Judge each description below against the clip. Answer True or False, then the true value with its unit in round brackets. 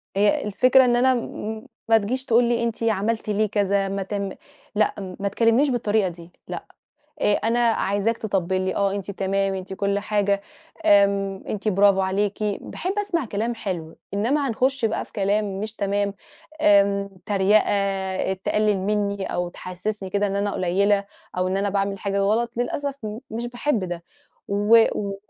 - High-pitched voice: True (205 Hz)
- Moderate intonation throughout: False (2.3 semitones)